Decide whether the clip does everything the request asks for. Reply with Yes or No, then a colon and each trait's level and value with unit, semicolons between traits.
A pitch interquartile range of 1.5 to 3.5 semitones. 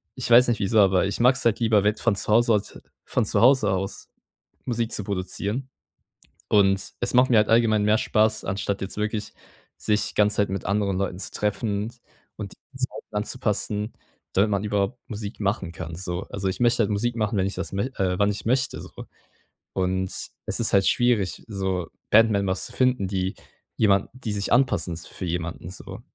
Yes: average, 2.7 semitones